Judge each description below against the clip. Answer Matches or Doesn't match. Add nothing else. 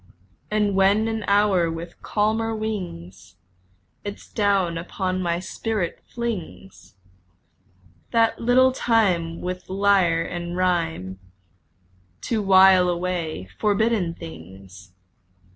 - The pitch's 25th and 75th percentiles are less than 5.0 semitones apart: Matches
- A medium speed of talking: Doesn't match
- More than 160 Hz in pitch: Matches